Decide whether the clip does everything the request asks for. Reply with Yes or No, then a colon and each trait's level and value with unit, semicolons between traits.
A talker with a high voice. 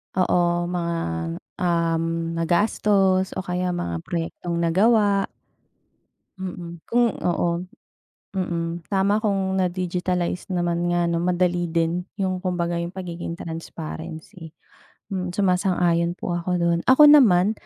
No: medium, 175 Hz